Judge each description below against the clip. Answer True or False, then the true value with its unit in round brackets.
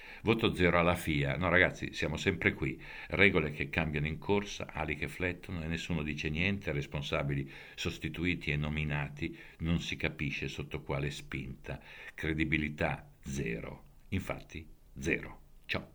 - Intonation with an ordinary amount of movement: True (3.0 semitones)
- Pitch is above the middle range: False (80 Hz)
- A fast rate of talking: False (135 wpm)